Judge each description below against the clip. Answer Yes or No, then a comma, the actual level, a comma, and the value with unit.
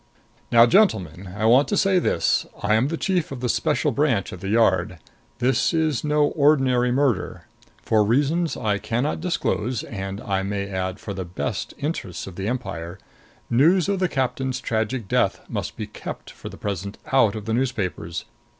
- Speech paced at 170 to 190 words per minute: Yes, average, 180 wpm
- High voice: No, low, 115 Hz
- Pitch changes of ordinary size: No, wide, 6.4 semitones